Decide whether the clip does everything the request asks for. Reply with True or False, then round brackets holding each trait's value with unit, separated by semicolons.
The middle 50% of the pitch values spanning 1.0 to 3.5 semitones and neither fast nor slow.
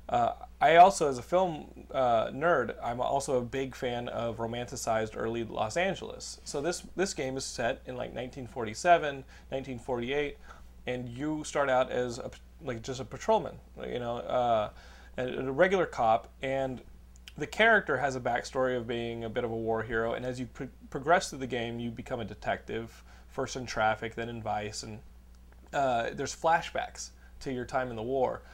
True (3.2 semitones; 185 wpm)